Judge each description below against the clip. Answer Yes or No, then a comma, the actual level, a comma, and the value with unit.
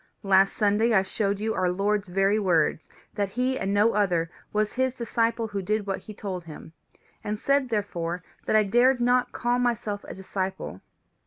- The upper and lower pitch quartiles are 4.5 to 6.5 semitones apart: No, average, 3.2 semitones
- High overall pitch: Yes, high, 205 Hz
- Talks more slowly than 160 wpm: No, average, 180 wpm